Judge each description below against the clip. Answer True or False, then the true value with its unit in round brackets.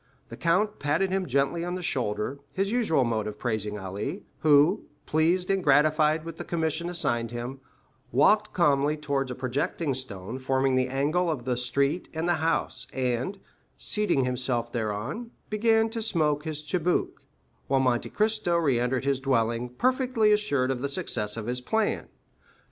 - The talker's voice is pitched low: False (145 Hz)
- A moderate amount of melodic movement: False (5.8 semitones)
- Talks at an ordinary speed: True (160 wpm)